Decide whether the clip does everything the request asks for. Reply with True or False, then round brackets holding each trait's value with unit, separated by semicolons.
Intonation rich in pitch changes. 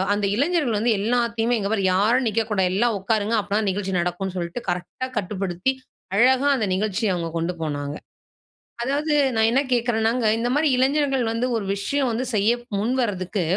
False (4.1 semitones)